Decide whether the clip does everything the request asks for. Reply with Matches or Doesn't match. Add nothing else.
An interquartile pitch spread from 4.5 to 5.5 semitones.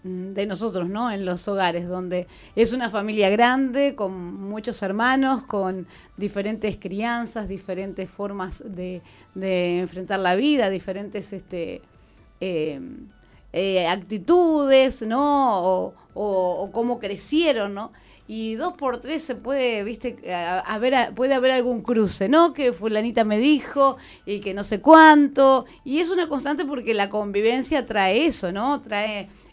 Matches